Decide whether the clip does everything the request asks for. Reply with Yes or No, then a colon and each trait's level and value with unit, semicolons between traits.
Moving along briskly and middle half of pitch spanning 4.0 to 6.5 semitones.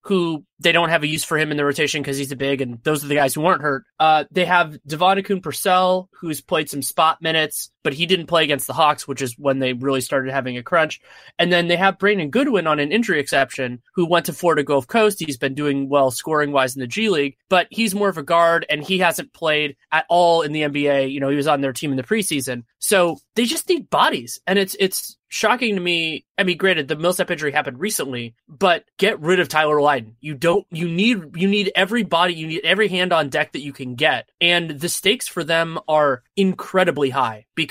Yes: fast, 240 wpm; average, 4.4 semitones